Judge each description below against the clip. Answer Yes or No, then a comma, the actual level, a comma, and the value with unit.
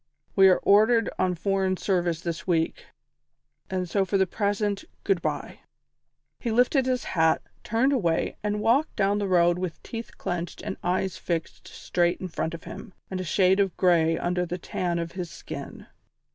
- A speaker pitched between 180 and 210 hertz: Yes, medium, 185 Hz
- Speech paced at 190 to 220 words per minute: No, average, 175 wpm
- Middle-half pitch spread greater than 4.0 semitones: No, average, 3.0 semitones